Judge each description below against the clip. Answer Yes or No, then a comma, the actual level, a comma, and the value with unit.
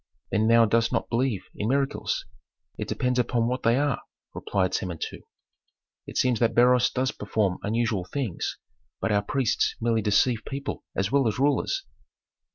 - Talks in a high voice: No, low, 115 Hz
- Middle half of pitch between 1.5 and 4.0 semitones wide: Yes, average, 3.3 semitones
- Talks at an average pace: Yes, average, 160 wpm